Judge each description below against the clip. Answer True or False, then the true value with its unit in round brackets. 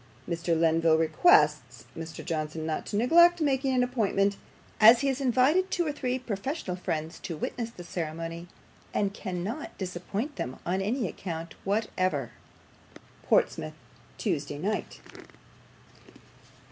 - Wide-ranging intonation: True (7.4 semitones)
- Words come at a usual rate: False (125 wpm)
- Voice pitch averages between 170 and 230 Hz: True (190 Hz)